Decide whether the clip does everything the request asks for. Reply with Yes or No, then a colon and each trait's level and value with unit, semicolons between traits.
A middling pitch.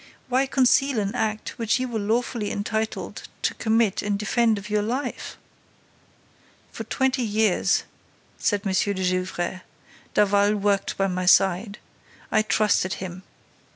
No: high, 210 Hz